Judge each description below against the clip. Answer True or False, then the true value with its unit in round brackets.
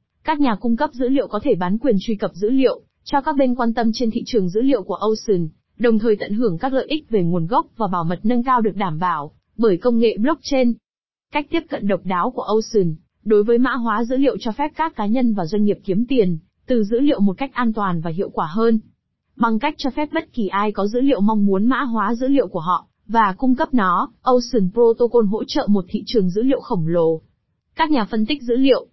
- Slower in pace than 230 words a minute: False (250 wpm)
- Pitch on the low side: False (230 Hz)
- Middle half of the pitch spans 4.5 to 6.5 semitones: False (4.1 semitones)